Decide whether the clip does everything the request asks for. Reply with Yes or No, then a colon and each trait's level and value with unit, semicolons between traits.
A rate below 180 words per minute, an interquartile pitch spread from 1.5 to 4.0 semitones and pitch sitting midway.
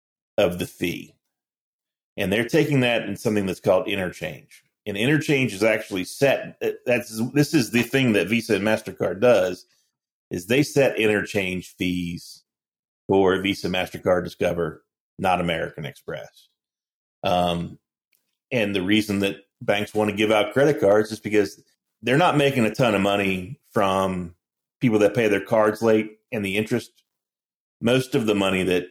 No: average, 160 wpm; average, 3.7 semitones; low, 105 Hz